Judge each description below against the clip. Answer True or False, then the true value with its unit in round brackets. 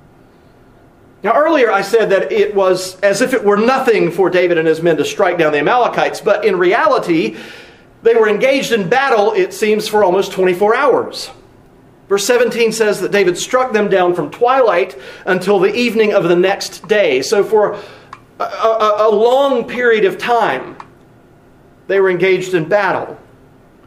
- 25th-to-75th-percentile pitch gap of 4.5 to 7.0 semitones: True (5.2 semitones)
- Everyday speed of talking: True (170 wpm)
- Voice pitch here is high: True (215 Hz)